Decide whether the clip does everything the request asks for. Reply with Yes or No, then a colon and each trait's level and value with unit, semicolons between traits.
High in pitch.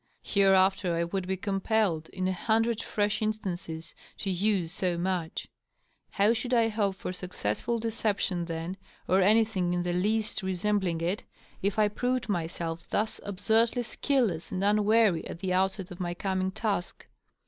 Yes: high, 195 Hz